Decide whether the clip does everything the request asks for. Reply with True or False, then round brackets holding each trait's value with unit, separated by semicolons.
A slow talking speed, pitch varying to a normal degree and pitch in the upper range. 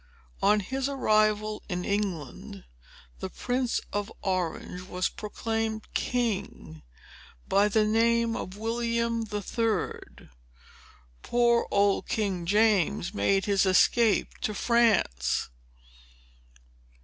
True (100 wpm; 3.0 semitones; 210 Hz)